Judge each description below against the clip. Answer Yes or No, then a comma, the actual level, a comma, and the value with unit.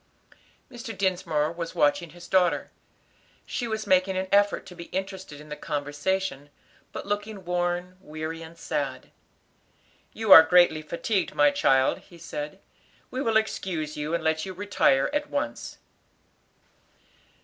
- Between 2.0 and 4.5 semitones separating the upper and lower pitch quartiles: Yes, average, 3.9 semitones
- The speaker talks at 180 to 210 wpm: No, average, 140 wpm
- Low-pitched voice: No, medium, 175 Hz